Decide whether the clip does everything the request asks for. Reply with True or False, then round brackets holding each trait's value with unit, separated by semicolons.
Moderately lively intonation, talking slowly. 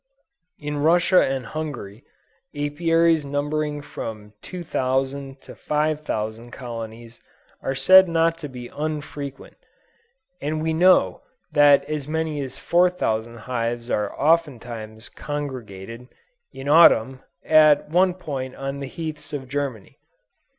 True (4.2 semitones; 115 wpm)